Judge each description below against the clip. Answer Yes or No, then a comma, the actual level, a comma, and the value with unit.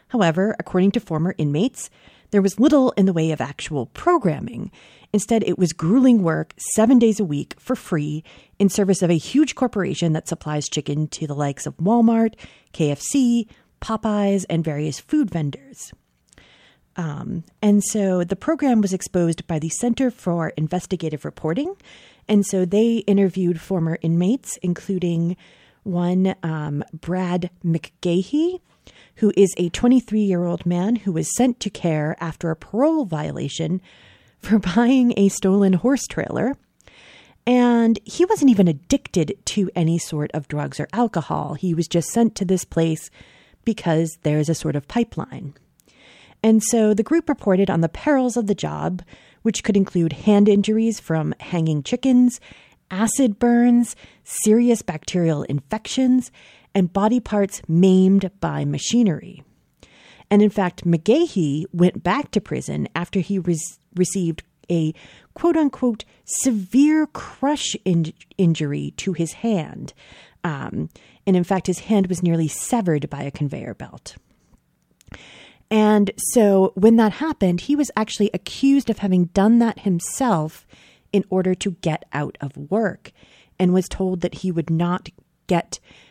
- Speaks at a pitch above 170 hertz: Yes, high, 190 Hz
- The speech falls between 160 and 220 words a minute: No, average, 145 wpm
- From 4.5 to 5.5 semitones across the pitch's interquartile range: Yes, average, 5.2 semitones